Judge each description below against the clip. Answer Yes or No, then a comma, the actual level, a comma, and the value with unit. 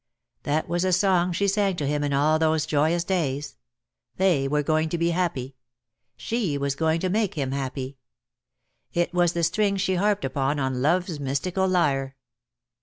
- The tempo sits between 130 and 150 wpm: No, average, 175 wpm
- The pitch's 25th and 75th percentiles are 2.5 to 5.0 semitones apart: Yes, average, 4.6 semitones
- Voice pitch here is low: No, medium, 160 Hz